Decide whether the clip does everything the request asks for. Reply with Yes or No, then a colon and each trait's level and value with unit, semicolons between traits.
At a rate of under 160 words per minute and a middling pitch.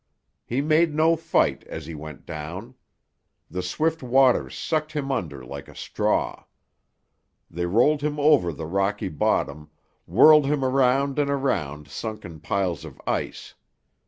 No: average, 140 wpm; low, 120 Hz